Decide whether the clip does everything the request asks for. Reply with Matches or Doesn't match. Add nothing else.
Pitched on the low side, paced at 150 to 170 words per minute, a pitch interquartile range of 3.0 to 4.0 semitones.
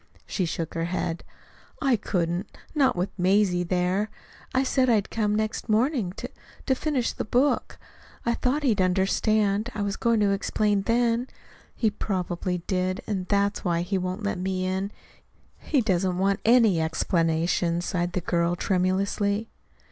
Doesn't match